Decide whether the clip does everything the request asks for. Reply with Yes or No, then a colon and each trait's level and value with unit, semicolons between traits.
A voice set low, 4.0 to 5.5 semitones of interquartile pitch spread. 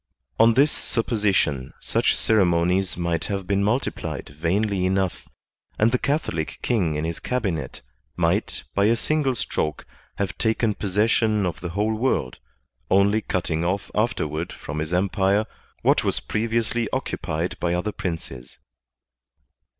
Yes: low, 100 Hz; average, 4.6 semitones